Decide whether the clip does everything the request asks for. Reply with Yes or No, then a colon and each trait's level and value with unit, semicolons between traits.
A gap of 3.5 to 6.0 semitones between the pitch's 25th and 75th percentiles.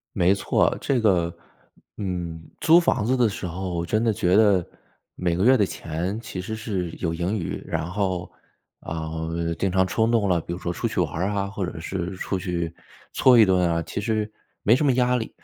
Yes: average, 3.9 semitones